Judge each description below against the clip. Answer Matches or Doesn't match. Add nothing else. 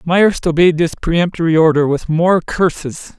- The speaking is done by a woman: Doesn't match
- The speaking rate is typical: Matches